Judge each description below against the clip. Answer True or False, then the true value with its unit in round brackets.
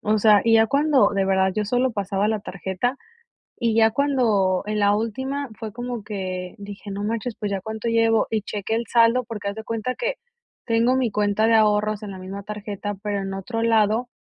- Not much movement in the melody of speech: True (2.3 semitones)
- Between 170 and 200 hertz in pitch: False (215 Hz)